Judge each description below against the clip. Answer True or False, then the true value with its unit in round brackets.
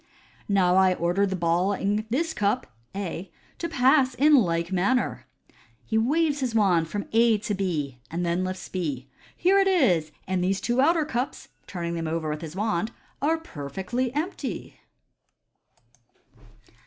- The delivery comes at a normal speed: True (170 wpm)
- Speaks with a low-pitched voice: False (200 Hz)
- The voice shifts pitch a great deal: True (6.9 semitones)